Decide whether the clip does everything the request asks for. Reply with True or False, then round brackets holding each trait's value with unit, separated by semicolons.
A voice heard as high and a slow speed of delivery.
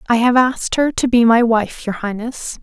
False (235 Hz; 230 wpm)